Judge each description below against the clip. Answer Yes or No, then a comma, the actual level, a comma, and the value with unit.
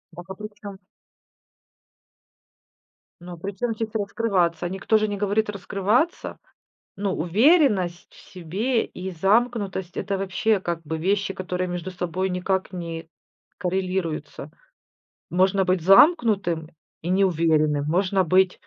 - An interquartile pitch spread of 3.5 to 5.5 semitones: No, average, 2.7 semitones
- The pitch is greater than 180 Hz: Yes, high, 190 Hz